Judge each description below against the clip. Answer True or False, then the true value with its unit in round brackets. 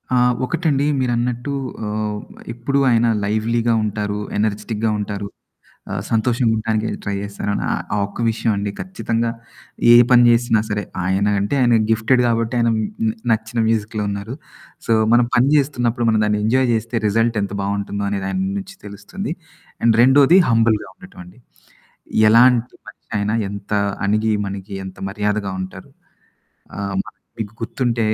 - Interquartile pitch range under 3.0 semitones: True (2.6 semitones)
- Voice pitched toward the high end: False (110 Hz)